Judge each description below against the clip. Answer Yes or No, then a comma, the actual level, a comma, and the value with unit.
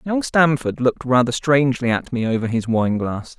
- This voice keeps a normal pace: Yes, average, 195 wpm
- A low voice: Yes, low, 130 Hz